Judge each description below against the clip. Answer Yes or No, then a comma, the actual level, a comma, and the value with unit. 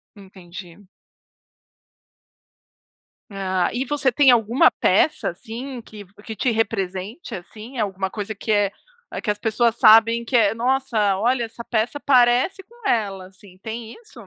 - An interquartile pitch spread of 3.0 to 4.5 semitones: Yes, average, 3.6 semitones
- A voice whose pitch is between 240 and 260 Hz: No, high, 225 Hz